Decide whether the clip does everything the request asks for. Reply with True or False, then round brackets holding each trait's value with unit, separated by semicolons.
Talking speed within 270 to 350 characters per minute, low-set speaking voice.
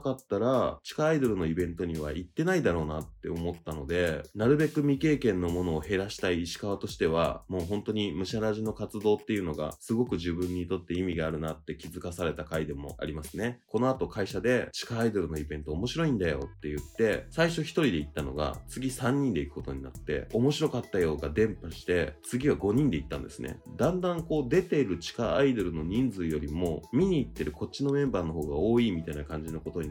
False (440 characters per minute; 90 Hz)